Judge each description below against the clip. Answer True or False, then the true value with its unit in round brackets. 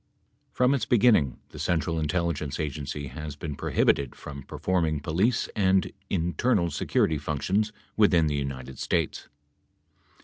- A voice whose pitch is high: False (80 Hz)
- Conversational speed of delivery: False (130 wpm)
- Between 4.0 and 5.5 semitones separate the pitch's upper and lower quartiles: True (4.6 semitones)